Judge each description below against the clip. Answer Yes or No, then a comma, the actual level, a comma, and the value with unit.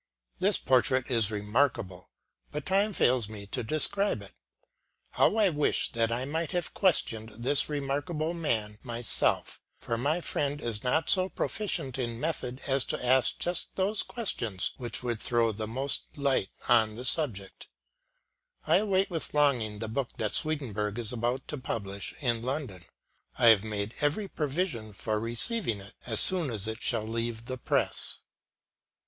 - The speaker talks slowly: No, average, 160 wpm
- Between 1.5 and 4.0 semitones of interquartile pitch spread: No, average, 5.3 semitones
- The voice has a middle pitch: No, low, 125 Hz